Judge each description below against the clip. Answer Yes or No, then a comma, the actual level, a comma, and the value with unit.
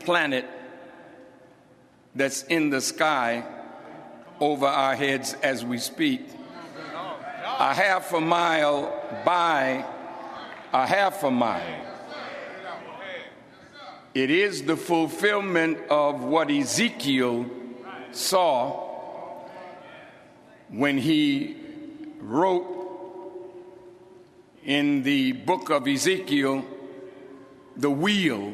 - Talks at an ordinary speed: No, slow, 80 wpm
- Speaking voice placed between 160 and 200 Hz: Yes, medium, 185 Hz